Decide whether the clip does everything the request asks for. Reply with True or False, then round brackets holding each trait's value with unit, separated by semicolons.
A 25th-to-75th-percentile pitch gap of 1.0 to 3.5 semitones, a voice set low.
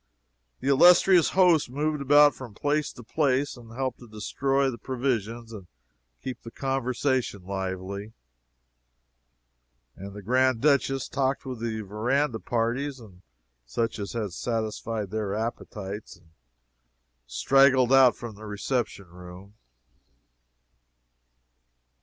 False (4.5 semitones; 120 Hz)